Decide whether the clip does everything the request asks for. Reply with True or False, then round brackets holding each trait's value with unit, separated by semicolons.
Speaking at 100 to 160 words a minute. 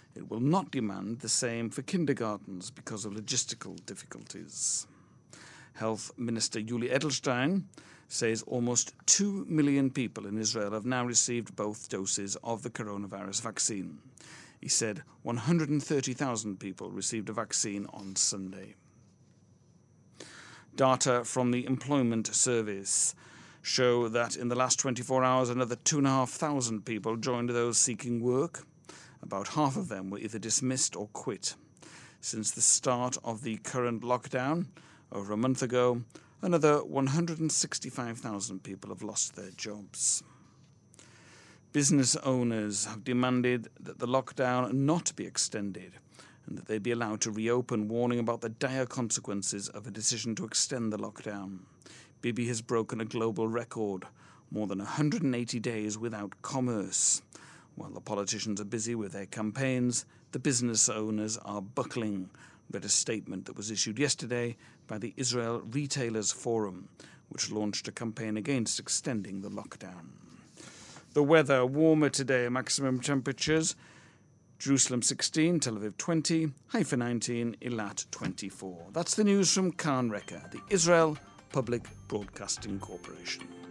True (140 wpm)